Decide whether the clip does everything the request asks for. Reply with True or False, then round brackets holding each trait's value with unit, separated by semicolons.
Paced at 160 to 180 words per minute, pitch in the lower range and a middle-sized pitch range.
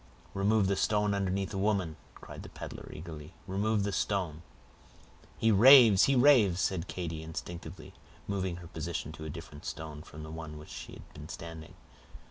True (170 wpm; 90 Hz; 4.1 semitones)